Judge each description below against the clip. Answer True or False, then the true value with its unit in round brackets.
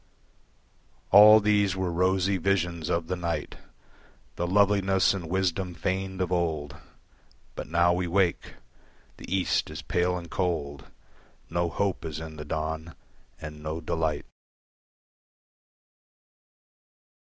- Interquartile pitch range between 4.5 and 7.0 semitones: False (2.8 semitones)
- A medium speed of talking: False (120 wpm)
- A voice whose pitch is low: True (85 Hz)